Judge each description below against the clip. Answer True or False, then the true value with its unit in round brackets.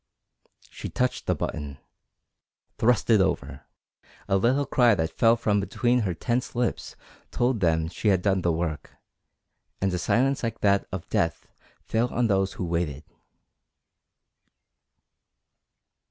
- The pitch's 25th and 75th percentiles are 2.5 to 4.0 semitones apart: False (5.5 semitones)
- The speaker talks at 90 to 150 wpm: True (135 wpm)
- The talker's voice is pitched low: True (100 Hz)